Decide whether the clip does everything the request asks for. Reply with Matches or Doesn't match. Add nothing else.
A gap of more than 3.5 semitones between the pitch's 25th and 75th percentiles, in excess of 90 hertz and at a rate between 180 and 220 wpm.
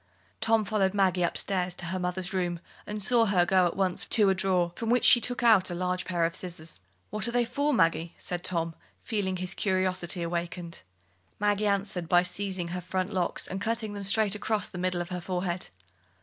Doesn't match